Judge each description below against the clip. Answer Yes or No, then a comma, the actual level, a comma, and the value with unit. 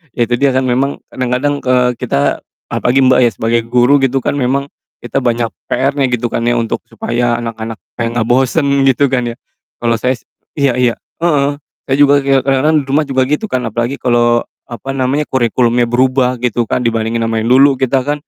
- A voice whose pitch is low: Yes, low, 125 Hz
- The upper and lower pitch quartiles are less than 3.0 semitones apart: Yes, narrow, 2.5 semitones